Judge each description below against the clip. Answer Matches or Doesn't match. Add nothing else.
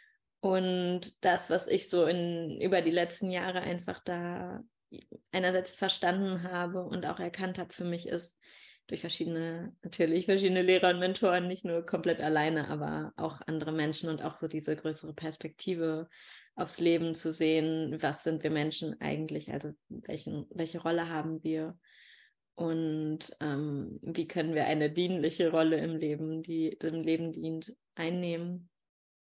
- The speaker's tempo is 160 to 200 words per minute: Doesn't match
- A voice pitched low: Doesn't match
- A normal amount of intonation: Doesn't match